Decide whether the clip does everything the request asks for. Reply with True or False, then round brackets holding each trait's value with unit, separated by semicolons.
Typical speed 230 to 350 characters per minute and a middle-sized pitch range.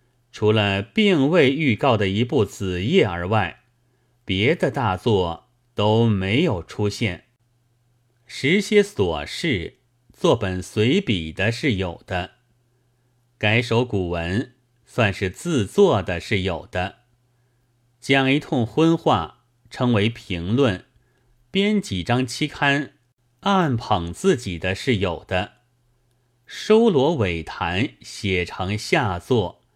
False (155 characters per minute; 3.7 semitones)